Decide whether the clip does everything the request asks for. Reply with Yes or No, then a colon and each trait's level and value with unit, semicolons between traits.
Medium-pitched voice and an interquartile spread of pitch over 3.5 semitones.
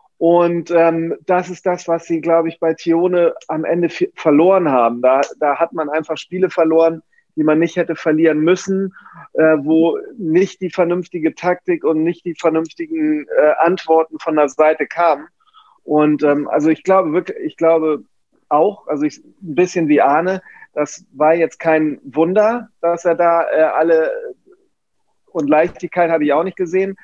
No: medium, 170 Hz; average, 2.7 semitones